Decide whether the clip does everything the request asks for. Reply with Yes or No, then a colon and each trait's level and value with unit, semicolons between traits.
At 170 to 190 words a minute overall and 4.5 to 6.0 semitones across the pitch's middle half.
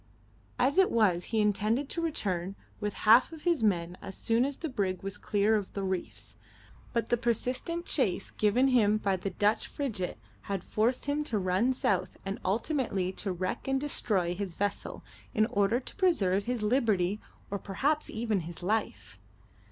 Yes: average, 175 wpm; average, 4.8 semitones